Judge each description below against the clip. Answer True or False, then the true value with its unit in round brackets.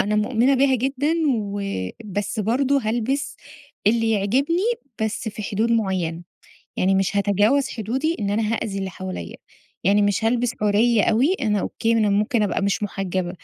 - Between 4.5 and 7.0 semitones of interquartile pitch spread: False (3.3 semitones)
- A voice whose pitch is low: False (215 Hz)